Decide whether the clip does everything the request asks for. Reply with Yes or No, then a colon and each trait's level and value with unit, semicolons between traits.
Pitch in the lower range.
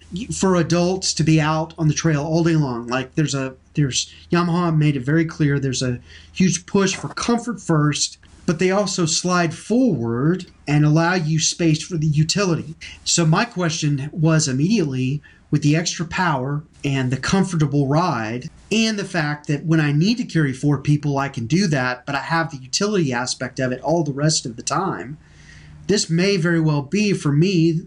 No: medium, 160 Hz